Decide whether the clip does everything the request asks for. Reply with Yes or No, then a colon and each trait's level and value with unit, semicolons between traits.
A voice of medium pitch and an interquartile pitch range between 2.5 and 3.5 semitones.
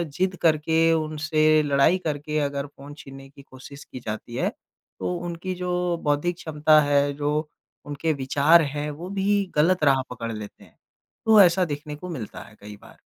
Yes: medium, 150 Hz; average, 3.2 semitones